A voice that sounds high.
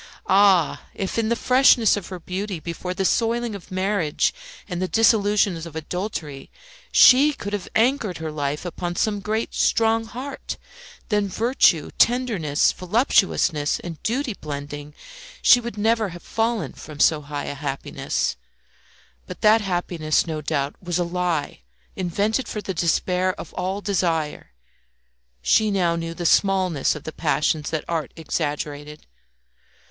No: medium, 180 Hz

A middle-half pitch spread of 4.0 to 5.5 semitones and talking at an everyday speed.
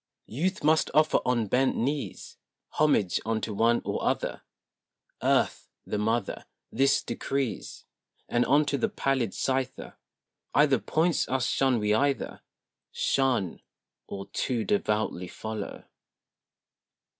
No: average, 4.3 semitones; slow, 115 wpm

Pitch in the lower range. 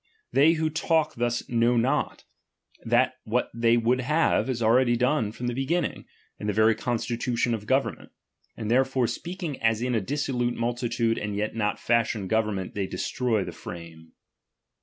Yes: low, 120 Hz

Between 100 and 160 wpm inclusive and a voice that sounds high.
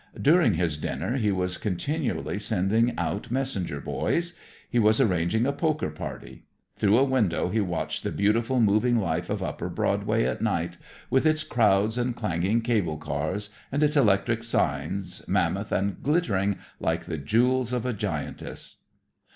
No: average, 155 wpm; low, 110 Hz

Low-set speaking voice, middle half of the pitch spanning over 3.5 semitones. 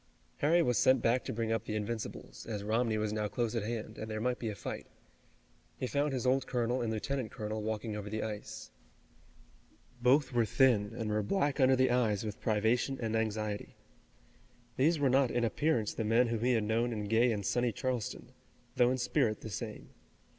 No: low, 115 Hz; narrow, 2.6 semitones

